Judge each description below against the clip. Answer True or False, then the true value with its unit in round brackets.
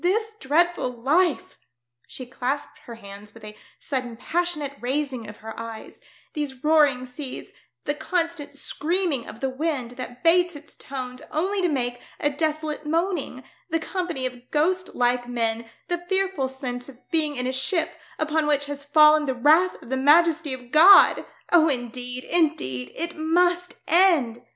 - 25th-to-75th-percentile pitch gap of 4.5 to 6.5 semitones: True (4.8 semitones)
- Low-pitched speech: False (290 Hz)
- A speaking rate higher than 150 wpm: True (165 wpm)